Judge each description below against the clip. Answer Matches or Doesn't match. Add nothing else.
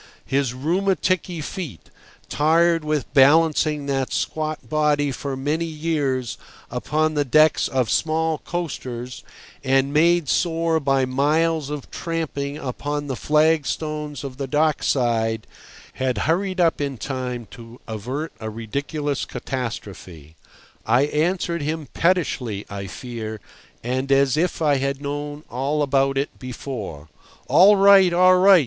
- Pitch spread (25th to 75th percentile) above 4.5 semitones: Doesn't match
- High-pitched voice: Doesn't match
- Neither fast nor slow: Doesn't match